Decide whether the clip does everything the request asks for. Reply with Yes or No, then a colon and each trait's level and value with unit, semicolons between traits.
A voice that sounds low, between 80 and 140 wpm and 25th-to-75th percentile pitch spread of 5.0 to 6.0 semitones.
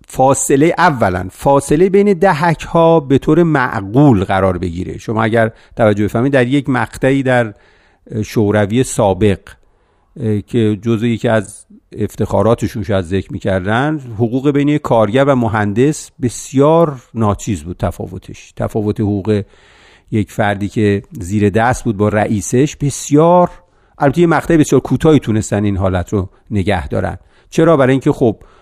Yes: low, 115 Hz; average, 135 wpm; wide, 5.4 semitones